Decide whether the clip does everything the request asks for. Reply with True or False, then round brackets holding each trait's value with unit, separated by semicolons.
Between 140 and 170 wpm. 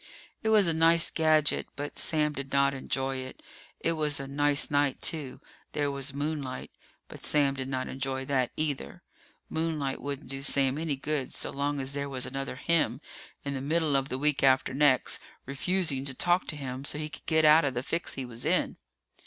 False (200 wpm)